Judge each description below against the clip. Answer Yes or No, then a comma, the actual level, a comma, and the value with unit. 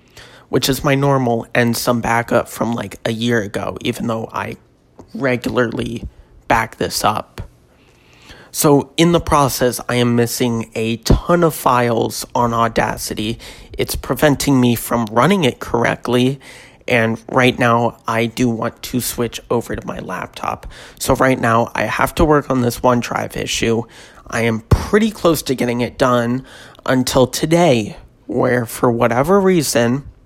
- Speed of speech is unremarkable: Yes, average, 150 wpm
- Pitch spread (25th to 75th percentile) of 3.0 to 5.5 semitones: No, narrow, 2.4 semitones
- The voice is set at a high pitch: No, low, 120 Hz